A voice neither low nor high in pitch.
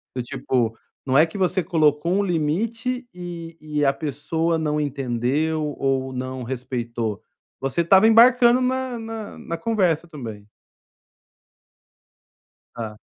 Yes: medium, 155 Hz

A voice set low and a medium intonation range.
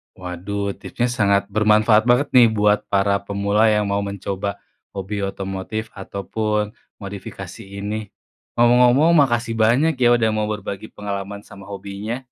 No: low, 105 Hz; narrow, 2.1 semitones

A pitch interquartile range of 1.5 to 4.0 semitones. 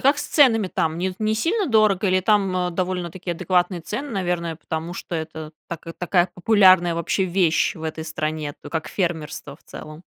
Yes: average, 3.1 semitones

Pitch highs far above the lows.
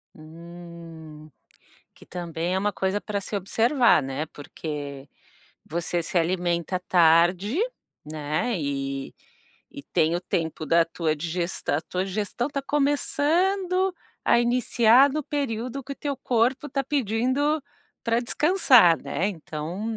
Yes: wide, 7.5 semitones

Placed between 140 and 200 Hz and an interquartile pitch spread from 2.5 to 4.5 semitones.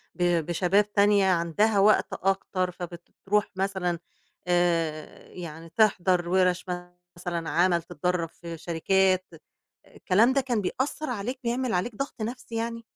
Yes: medium, 185 Hz; average, 3.2 semitones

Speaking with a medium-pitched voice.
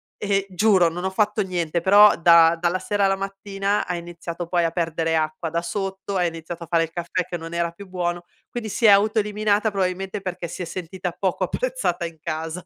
Yes: medium, 180 Hz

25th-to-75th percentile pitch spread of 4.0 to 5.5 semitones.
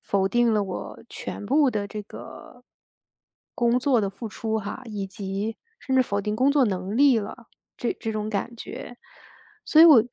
No: average, 3.5 semitones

